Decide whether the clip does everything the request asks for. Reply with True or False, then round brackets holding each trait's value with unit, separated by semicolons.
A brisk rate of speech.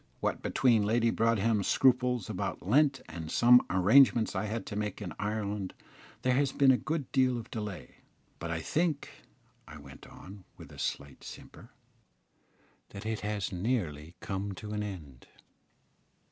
False (155 wpm)